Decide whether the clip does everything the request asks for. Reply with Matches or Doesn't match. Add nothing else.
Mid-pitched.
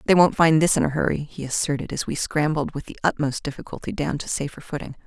Matches